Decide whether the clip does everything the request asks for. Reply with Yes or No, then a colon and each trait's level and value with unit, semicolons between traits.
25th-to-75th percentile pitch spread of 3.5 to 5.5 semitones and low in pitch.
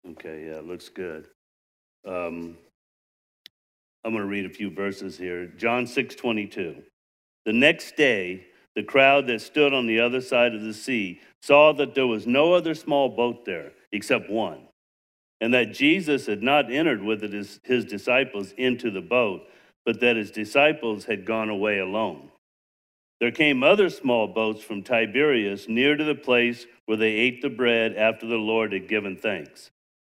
Yes: average, 4.3 semitones; low, 110 Hz